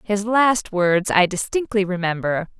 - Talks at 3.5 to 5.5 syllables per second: Yes, 4.1 syllables/s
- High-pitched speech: Yes, high, 200 Hz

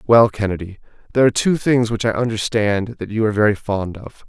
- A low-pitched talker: Yes, low, 110 Hz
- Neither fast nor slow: No, fast, 210 wpm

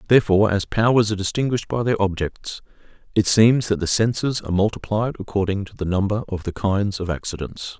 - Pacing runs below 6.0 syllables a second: No, 6.1 syllables/s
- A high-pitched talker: No, low, 105 Hz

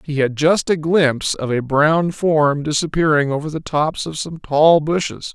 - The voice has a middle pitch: Yes, medium, 155 Hz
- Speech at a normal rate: Yes, average, 190 wpm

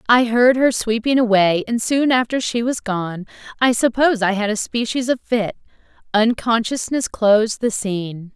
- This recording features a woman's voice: Yes, female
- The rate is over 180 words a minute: No, average, 165 wpm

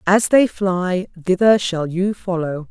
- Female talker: Yes, female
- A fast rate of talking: No, average, 155 wpm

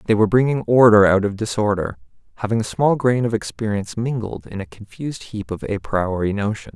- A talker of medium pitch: No, low, 105 Hz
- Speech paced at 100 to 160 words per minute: No, average, 195 wpm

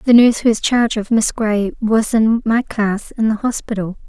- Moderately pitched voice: No, high, 220 Hz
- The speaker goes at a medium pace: No, fast, 220 wpm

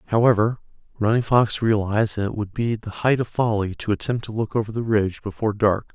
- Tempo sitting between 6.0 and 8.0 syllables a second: Yes, 6.1 syllables/s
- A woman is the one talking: No, male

